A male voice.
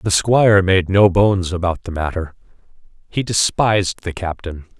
Yes: male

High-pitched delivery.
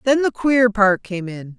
Yes: high, 220 Hz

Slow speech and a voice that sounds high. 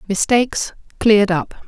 Yes: slow, 110 wpm; high, 210 Hz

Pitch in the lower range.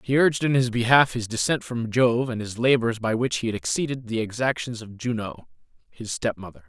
Yes: low, 120 Hz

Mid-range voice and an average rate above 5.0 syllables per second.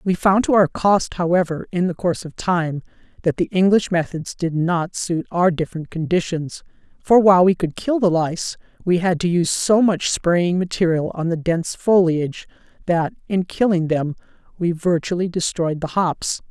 No: medium, 175 Hz; 4.9 syllables/s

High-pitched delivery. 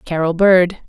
No: medium, 175 Hz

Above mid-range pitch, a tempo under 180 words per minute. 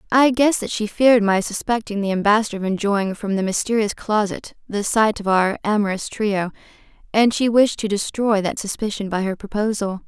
No: high, 210 Hz; average, 185 wpm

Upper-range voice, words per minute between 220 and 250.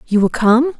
Yes: high, 240 Hz; fast, 225 wpm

